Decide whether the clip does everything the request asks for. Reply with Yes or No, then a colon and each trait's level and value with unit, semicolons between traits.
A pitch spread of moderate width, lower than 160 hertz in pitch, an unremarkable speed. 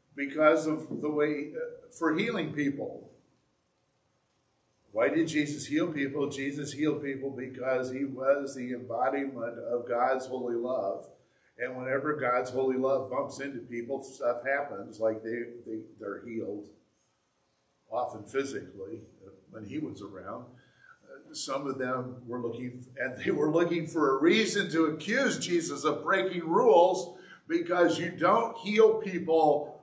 Yes: average, 4.1 semitones; medium, 140 Hz; average, 145 wpm